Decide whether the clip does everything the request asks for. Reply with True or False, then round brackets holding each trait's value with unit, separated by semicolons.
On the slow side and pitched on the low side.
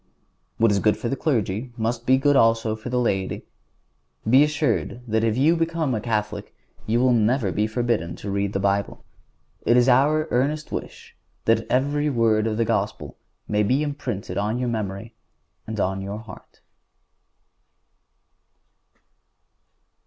False (155 wpm; 115 Hz)